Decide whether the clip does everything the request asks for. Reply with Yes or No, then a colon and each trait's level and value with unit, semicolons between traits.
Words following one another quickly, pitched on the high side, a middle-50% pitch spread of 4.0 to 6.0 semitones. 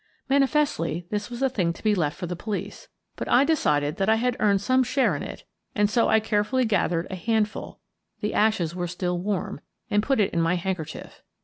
Yes: fast, 225 wpm; high, 210 Hz; average, 4.7 semitones